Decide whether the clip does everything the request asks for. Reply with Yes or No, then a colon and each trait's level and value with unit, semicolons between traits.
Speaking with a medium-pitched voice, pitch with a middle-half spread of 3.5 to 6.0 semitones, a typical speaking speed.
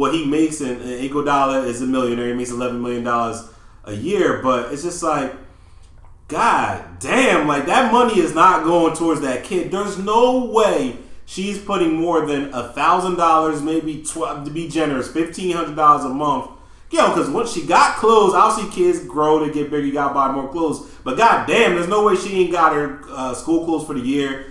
No: medium, 150 Hz; average, 4.8 semitones; fast, 215 wpm